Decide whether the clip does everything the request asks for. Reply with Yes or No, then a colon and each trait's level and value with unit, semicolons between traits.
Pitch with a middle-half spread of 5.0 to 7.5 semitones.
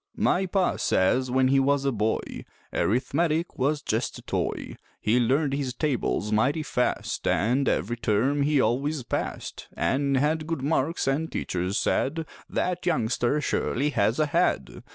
No: average, 4.1 semitones